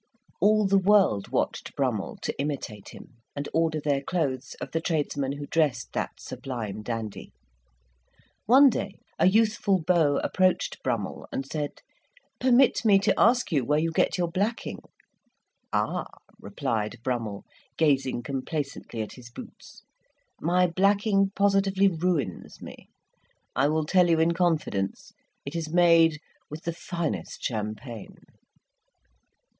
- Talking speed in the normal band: No, slow, 130 wpm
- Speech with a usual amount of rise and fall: No, wide, 5.9 semitones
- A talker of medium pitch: Yes, medium, 160 Hz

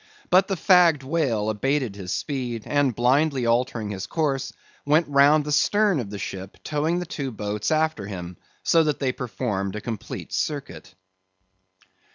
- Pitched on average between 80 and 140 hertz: Yes, low, 135 Hz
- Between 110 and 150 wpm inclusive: No, average, 160 wpm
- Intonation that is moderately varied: No, wide, 6.3 semitones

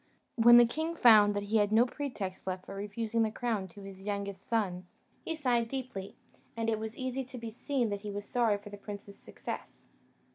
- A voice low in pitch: No, high, 220 Hz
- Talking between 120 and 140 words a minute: No, fast, 205 wpm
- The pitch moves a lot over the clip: No, average, 3.0 semitones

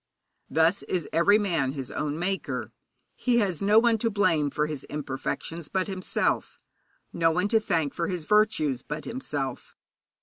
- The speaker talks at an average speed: Yes, average, 160 wpm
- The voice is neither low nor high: Yes, medium, 170 Hz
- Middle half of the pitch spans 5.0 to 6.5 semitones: Yes, average, 5.3 semitones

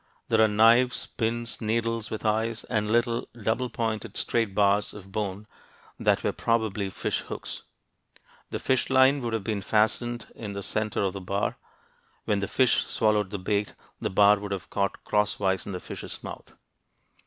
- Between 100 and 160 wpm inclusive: No, average, 175 wpm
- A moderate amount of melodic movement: No, narrow, 2.3 semitones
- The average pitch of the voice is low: Yes, low, 110 Hz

